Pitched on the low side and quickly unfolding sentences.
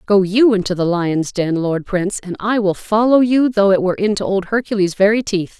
No: high, 200 Hz; fast, 225 wpm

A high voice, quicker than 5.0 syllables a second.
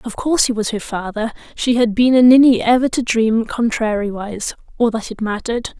Yes: high, 230 Hz; 5.5 syllables/s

